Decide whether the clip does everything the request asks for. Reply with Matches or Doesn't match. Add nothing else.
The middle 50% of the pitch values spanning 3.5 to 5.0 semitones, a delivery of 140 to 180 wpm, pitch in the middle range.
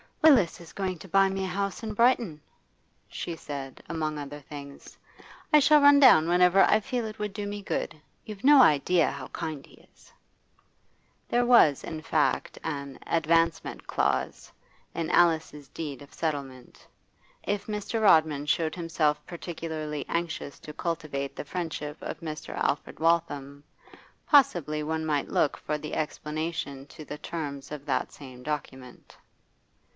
Matches